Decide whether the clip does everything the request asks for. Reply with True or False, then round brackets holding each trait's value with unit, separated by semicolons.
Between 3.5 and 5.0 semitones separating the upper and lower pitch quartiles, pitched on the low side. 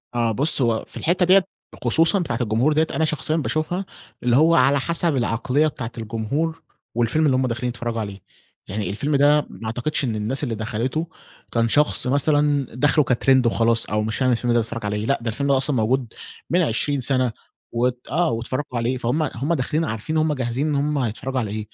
True (4.5 semitones; 130 Hz)